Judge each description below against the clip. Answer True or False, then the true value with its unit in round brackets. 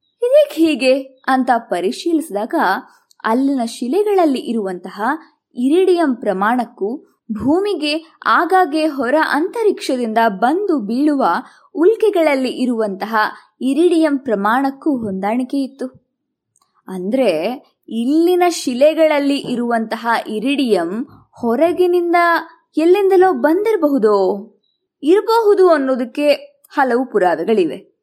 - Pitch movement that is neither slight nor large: False (6.0 semitones)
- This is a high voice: True (285 Hz)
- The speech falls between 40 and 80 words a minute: True (70 wpm)